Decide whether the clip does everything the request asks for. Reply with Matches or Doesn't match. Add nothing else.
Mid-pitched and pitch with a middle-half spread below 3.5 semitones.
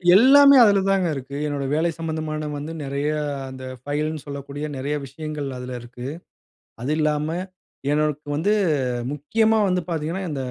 Matches